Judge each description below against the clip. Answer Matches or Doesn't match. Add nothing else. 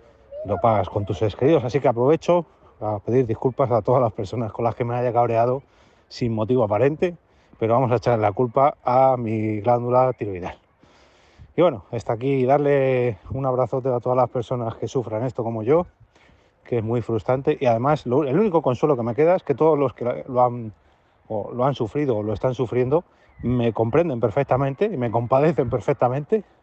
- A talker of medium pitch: Doesn't match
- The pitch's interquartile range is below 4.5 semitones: Matches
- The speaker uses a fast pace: Matches